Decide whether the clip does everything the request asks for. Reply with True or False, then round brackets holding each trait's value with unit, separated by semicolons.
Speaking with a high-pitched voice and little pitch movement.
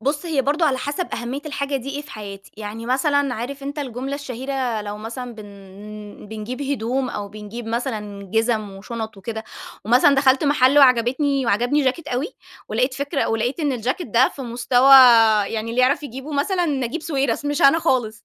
False (255 Hz; 3.8 semitones)